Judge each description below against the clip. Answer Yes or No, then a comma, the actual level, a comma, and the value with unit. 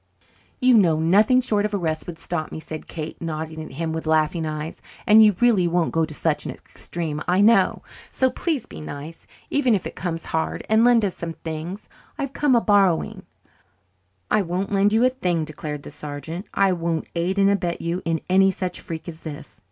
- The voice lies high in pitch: No, medium, 175 Hz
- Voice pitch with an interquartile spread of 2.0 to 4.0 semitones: No, average, 4.4 semitones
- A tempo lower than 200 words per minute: No, fast, 205 wpm